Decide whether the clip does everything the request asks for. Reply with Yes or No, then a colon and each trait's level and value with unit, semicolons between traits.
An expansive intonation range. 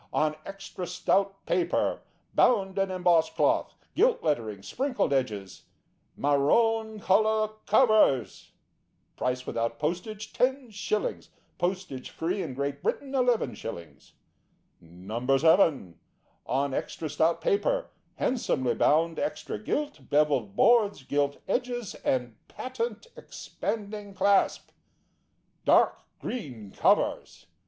Yes: wide, 8.3 semitones